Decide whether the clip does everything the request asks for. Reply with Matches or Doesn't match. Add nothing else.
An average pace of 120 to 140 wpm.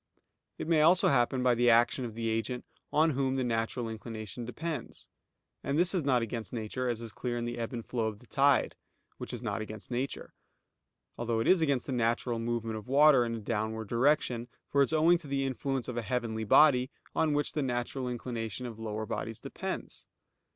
Doesn't match